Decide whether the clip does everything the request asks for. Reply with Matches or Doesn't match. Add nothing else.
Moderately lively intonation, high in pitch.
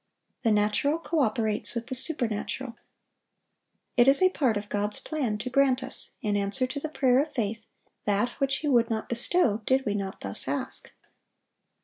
Matches